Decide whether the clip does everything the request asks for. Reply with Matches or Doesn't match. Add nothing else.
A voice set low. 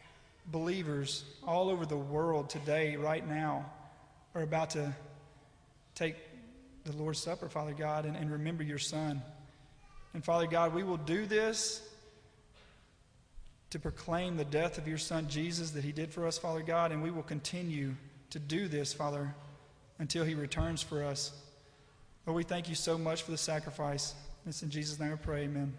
Doesn't match